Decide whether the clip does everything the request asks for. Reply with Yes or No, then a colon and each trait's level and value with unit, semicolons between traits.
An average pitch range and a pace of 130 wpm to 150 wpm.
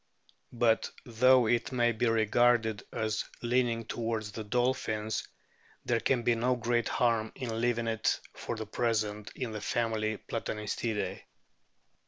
No: narrow, 1.7 semitones; slow, 135 wpm